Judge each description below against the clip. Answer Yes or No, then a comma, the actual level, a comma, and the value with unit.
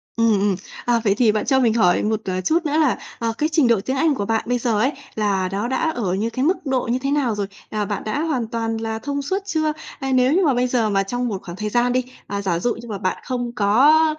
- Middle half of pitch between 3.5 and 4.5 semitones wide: Yes, average, 4.2 semitones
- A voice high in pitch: Yes, high, 235 Hz